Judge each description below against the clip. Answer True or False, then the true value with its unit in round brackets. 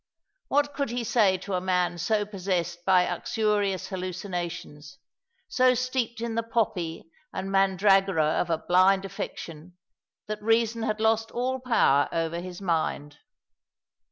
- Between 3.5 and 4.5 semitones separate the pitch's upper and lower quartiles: True (4.2 semitones)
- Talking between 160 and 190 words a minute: False (135 wpm)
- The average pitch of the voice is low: False (195 Hz)